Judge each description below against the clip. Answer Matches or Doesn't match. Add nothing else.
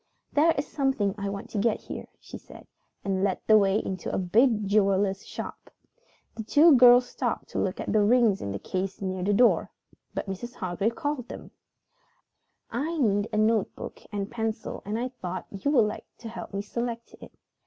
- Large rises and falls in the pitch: Doesn't match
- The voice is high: Matches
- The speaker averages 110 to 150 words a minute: Doesn't match